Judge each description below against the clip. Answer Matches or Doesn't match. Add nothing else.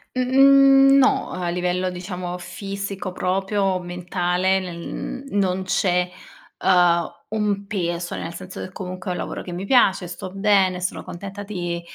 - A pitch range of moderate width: Doesn't match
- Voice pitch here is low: Doesn't match